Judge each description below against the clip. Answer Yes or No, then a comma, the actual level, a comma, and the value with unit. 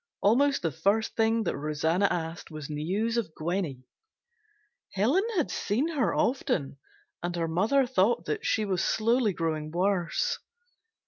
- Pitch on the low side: No, high, 195 Hz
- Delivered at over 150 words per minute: No, average, 140 wpm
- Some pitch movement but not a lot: No, wide, 5.9 semitones